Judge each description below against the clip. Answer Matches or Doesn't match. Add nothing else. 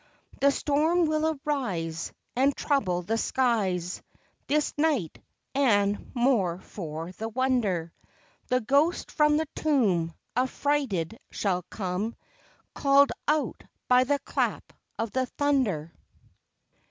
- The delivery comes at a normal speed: Doesn't match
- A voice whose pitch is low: Doesn't match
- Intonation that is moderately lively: Doesn't match